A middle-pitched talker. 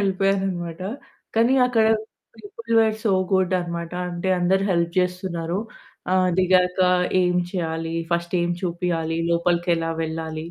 Yes: medium, 180 Hz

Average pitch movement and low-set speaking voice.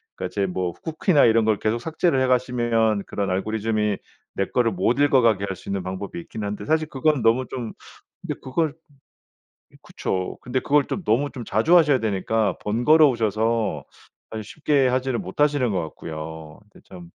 Yes: average, 4.8 semitones; low, 115 Hz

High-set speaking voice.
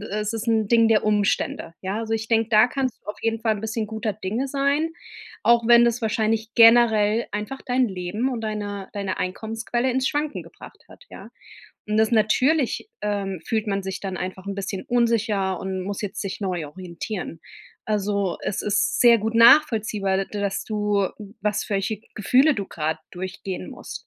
Yes: high, 215 Hz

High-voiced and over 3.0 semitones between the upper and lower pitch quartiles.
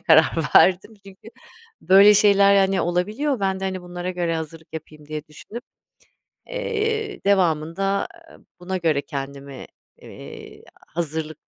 No: medium, 180 Hz; average, 3.9 semitones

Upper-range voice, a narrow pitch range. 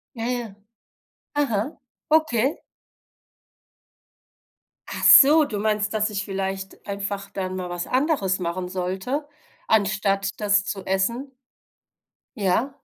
No: high, 205 Hz; average, 4.3 semitones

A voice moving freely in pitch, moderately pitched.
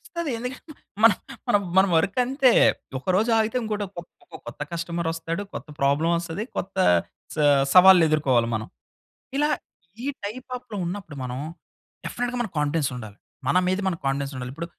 Yes: wide, 6.7 semitones; medium, 175 Hz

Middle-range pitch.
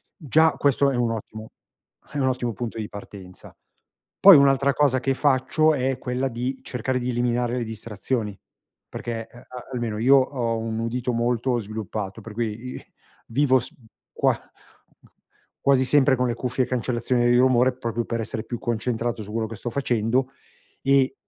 No: low, 120 Hz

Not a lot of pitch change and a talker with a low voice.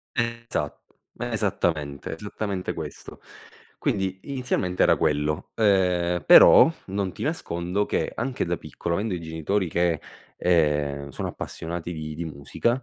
No: average, 4.3 semitones; very low, 90 Hz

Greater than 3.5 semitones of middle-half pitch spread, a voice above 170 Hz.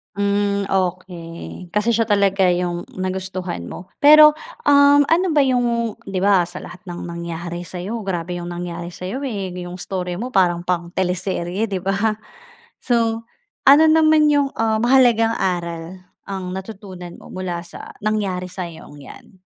Yes: average, 4.2 semitones; high, 190 Hz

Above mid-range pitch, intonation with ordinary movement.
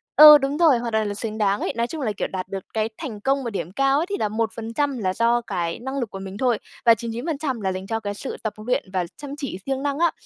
Yes: high, 230 Hz; average, 5.0 semitones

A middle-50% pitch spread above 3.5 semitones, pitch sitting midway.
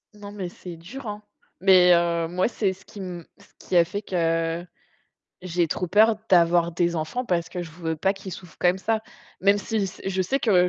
No: average, 2.8 semitones; medium, 180 Hz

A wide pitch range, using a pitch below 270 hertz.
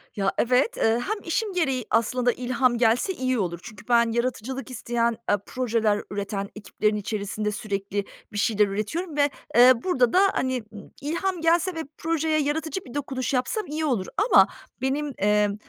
Yes: wide, 5.7 semitones; high, 245 Hz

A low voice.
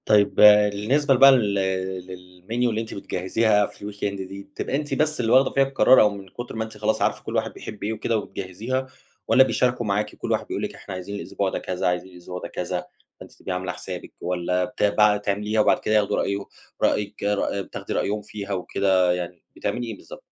Yes: low, 105 Hz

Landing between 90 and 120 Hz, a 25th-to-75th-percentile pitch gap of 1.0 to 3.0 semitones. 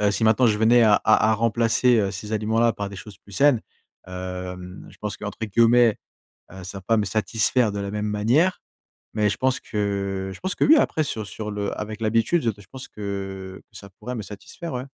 Yes: low, 105 Hz; narrow, 2.6 semitones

